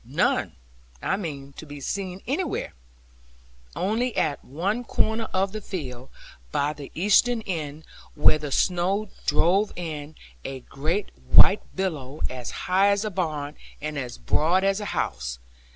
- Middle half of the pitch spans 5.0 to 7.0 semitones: Yes, wide, 5.5 semitones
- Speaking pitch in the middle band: Yes, medium, 170 Hz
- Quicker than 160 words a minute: No, average, 145 wpm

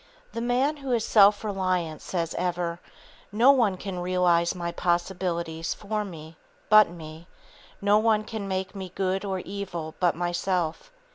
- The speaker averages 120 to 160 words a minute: Yes, average, 150 wpm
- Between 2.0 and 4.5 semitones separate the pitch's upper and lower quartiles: Yes, average, 3.4 semitones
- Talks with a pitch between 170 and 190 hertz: Yes, medium, 185 Hz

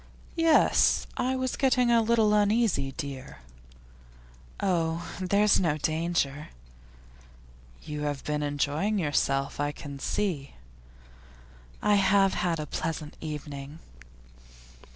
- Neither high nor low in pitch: Yes, medium, 165 Hz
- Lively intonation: Yes, wide, 6.2 semitones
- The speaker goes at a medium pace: No, slow, 105 wpm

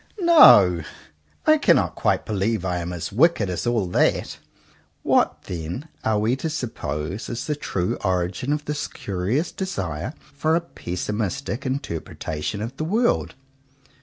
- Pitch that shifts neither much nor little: No, wide, 8.6 semitones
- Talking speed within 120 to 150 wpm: Yes, average, 140 wpm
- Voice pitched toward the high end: No, low, 110 Hz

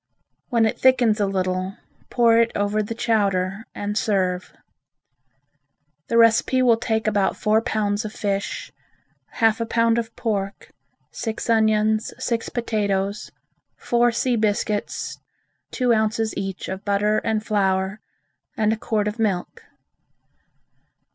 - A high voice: Yes, high, 215 Hz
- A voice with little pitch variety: Yes, narrow, 2.1 semitones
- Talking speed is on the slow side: Yes, slow, 130 wpm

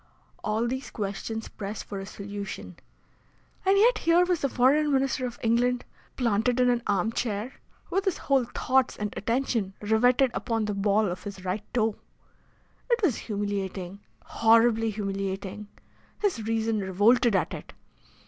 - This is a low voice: No, high, 225 Hz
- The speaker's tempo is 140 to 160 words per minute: Yes, average, 150 wpm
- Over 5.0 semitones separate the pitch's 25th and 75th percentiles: No, average, 3.8 semitones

